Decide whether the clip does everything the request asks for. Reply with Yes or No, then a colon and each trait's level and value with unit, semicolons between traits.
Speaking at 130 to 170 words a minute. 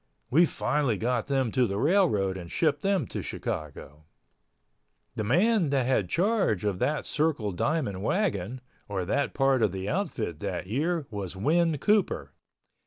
Yes: average, 155 wpm